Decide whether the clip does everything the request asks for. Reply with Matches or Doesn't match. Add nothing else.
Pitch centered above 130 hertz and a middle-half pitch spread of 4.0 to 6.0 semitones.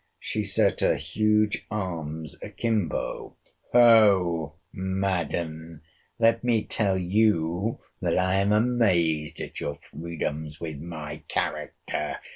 Doesn't match